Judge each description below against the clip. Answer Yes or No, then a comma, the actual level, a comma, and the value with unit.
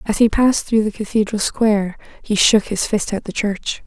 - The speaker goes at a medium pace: No, fast, 215 wpm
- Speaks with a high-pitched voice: Yes, high, 210 Hz